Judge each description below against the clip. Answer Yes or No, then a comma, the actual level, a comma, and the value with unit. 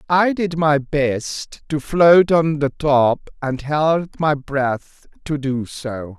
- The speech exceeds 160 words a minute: No, average, 155 wpm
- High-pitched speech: No, medium, 145 Hz